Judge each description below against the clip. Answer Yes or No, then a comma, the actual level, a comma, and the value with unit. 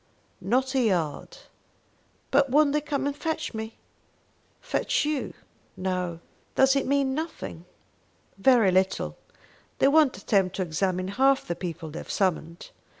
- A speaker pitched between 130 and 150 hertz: No, high, 225 Hz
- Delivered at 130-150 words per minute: Yes, average, 140 wpm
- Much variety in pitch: Yes, wide, 7.3 semitones